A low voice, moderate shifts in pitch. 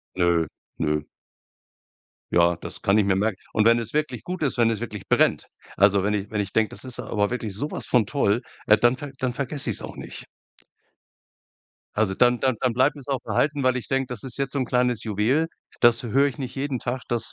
Yes: low, 120 Hz; average, 4.2 semitones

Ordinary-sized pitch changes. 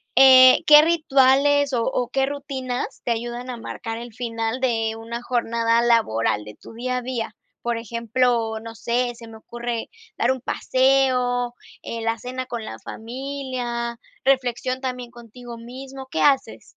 No: narrow, 2.0 semitones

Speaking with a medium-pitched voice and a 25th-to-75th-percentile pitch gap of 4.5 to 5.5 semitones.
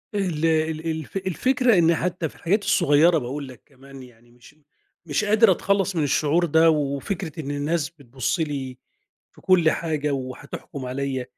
No: medium, 155 Hz; average, 3.9 semitones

